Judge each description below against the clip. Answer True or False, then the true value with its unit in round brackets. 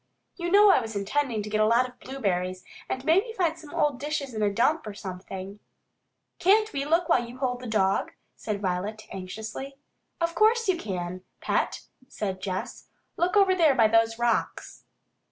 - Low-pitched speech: False (240 Hz)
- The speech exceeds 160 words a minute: True (185 wpm)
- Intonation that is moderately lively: False (7.9 semitones)